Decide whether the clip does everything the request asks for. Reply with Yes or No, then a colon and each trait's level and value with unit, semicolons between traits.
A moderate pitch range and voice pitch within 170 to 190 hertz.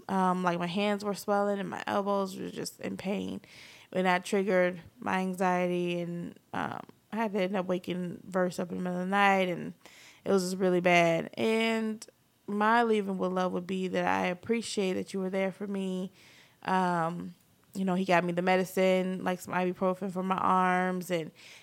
No: narrow, 1.7 semitones; medium, 185 Hz